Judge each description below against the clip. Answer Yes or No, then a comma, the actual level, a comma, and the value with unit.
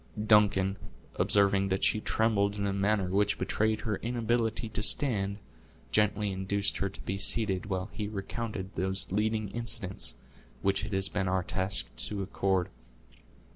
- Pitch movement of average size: No, narrow, 1.9 semitones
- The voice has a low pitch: Yes, low, 100 Hz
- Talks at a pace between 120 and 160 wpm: Yes, average, 150 wpm